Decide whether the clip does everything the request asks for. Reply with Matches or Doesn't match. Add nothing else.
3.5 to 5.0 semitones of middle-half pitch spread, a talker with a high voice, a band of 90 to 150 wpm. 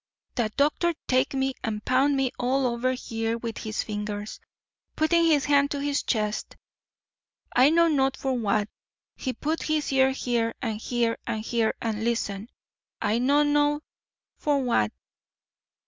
Matches